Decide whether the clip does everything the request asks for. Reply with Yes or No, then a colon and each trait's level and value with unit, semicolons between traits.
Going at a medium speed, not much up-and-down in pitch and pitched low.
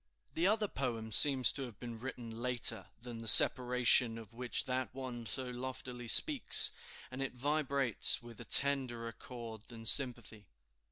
Yes: average, 155 wpm; narrow, 2.2 semitones; low, 125 Hz